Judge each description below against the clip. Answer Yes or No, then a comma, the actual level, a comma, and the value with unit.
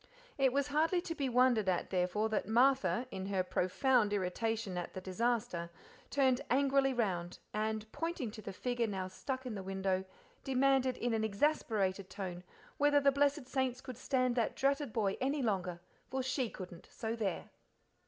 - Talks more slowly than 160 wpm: No, average, 170 wpm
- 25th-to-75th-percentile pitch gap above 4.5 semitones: Yes, wide, 5.5 semitones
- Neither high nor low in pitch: No, high, 230 Hz